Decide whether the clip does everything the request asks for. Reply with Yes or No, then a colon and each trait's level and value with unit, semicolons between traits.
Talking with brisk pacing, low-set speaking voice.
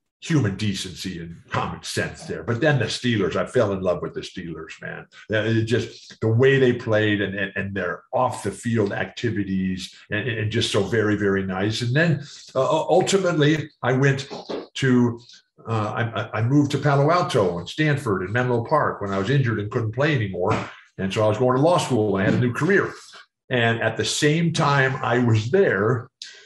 No: average, 195 wpm; low, 120 Hz